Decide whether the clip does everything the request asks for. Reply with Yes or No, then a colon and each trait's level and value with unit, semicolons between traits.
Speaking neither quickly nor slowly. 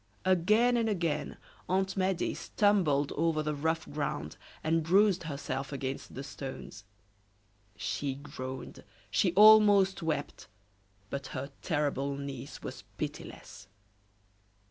No: slow, 110 wpm